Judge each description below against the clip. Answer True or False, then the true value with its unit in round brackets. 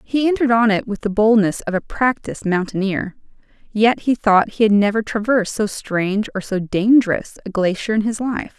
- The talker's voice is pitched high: True (215 Hz)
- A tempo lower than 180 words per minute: False (195 wpm)